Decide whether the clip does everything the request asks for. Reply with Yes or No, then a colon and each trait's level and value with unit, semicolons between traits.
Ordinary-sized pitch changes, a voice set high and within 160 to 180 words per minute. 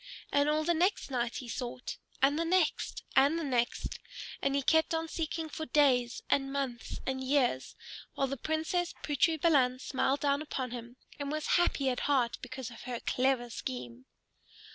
Yes: average, 3.7 semitones; very high, 275 Hz; average, 175 wpm